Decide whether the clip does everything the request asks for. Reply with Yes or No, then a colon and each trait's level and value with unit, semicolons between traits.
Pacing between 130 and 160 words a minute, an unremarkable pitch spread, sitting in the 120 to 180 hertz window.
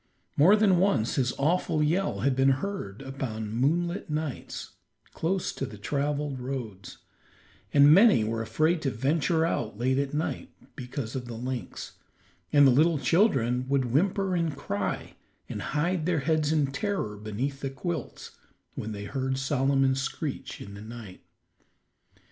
Yes: average, 150 wpm; average, 4.7 semitones; low, 135 Hz